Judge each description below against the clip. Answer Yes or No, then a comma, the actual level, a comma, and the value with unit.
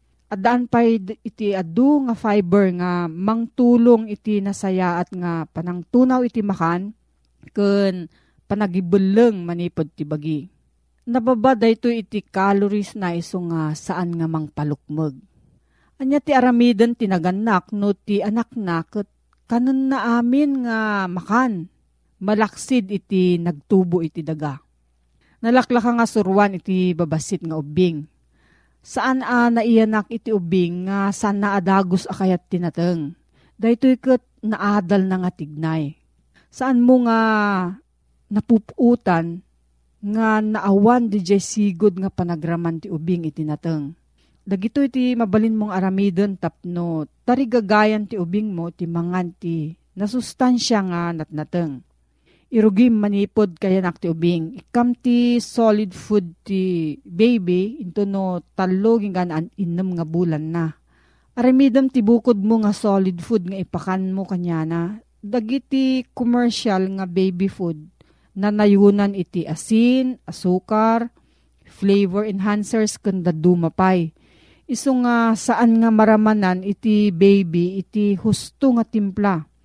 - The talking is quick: No, average, 120 wpm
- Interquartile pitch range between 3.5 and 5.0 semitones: Yes, average, 4.4 semitones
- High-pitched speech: Yes, high, 200 Hz